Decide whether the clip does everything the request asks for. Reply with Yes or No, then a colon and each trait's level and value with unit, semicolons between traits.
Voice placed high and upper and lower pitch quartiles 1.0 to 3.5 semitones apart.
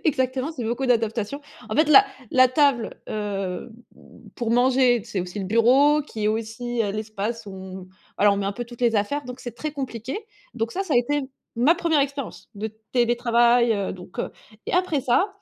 No: high, 240 Hz; average, 4.1 semitones